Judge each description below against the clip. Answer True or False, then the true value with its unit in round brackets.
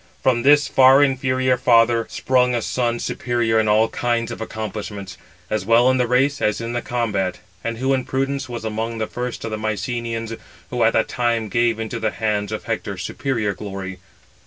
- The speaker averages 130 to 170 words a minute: False (190 wpm)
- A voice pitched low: True (115 Hz)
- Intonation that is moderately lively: False (2.3 semitones)